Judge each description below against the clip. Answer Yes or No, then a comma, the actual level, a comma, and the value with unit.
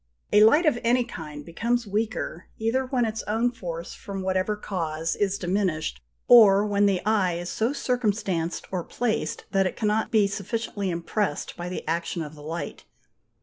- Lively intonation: No, average, 4.4 semitones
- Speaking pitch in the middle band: No, high, 200 Hz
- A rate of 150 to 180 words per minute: Yes, average, 170 wpm